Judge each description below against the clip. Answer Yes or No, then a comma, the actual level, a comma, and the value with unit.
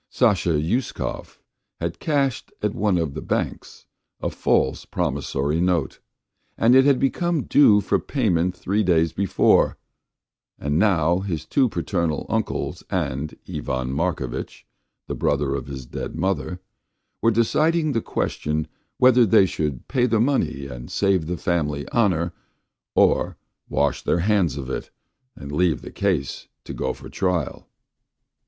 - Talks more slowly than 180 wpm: Yes, average, 140 wpm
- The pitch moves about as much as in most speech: No, wide, 6.5 semitones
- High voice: No, very low, 90 Hz